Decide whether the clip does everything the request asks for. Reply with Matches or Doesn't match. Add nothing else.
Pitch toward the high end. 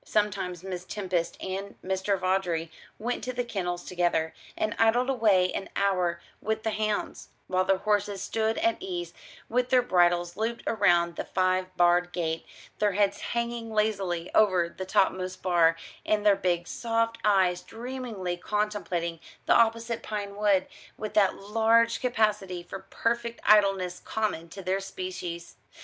Matches